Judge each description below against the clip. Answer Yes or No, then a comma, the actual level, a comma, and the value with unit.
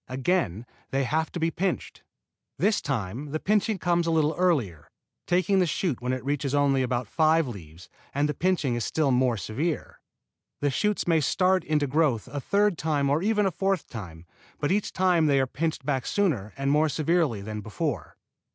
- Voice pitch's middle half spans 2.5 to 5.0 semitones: No, wide, 5.4 semitones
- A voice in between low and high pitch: Yes, medium, 150 Hz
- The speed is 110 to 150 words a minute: No, average, 190 wpm